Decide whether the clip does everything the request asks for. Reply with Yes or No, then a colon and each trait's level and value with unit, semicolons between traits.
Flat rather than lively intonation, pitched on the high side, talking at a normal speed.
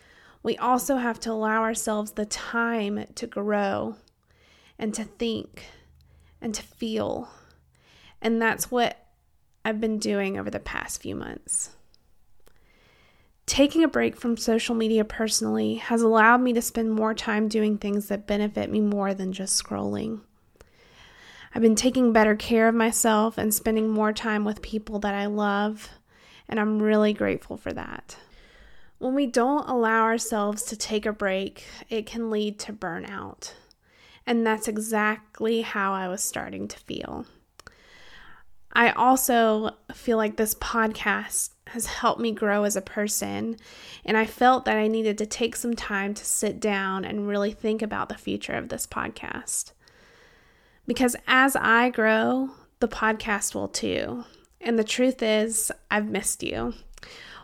Yes: narrow, 1.8 semitones; high, 220 Hz; average, 150 wpm